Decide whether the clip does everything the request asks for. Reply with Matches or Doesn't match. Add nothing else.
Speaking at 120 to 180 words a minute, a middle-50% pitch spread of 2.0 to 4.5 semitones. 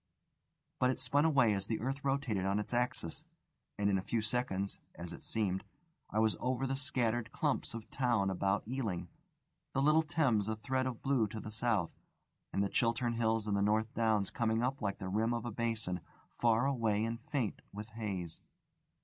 Doesn't match